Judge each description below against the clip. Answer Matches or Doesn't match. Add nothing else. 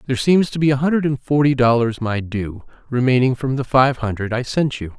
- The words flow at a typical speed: Doesn't match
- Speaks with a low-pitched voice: Matches